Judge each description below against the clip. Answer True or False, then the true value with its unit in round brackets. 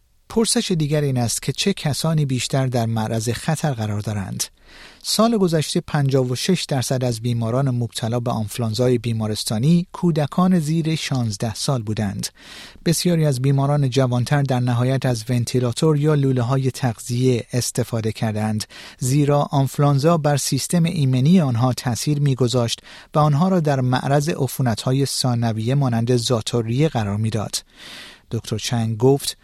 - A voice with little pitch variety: False (3.9 semitones)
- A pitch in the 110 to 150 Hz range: True (130 Hz)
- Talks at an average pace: True (130 wpm)